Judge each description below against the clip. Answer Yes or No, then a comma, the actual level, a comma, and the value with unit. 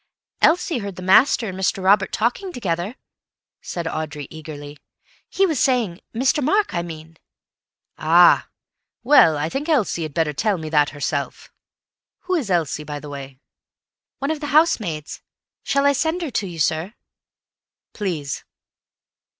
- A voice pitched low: No, medium, 185 Hz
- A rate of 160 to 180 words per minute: No, average, 145 wpm